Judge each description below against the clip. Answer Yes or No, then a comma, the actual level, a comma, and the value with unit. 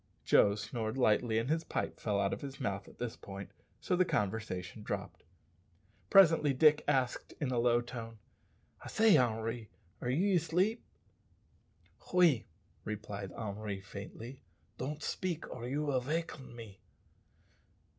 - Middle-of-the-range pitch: No, low, 120 Hz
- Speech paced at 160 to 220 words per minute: No, average, 140 wpm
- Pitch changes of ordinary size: No, wide, 5.9 semitones